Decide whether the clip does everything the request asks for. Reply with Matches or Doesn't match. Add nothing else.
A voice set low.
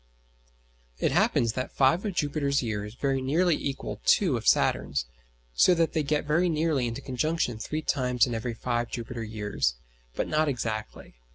Matches